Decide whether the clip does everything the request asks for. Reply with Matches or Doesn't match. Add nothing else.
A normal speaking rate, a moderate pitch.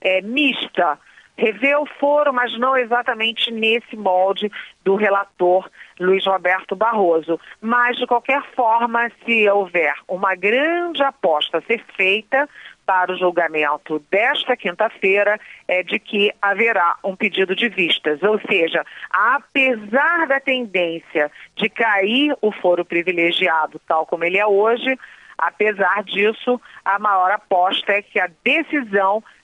Doesn't match